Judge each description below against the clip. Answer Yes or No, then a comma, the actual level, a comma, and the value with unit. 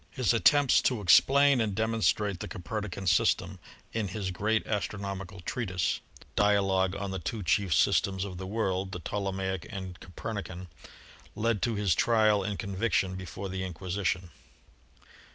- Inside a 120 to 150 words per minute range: Yes, average, 145 wpm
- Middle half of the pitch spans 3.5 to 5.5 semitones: No, narrow, 2.4 semitones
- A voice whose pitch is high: No, low, 100 Hz